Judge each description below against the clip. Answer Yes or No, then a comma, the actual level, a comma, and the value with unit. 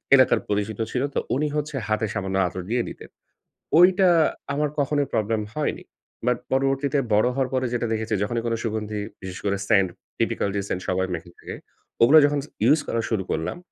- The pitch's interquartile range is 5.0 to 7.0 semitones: Yes, average, 5.3 semitones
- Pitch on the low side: Yes, low, 115 Hz